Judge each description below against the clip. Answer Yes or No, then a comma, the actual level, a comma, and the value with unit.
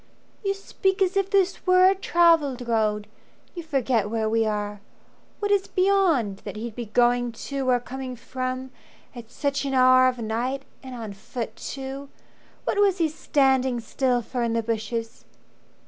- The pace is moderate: Yes, average, 165 wpm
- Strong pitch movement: Yes, wide, 5.8 semitones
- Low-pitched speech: No, very high, 255 Hz